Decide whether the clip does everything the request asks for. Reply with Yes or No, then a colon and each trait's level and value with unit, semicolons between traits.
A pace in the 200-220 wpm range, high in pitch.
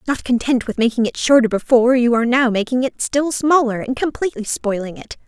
Yes: fast, 205 wpm; high, 245 Hz